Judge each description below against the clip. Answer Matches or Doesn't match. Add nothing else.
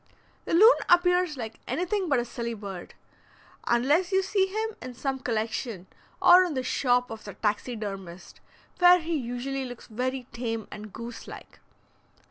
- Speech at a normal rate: Matches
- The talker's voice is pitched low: Doesn't match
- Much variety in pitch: Matches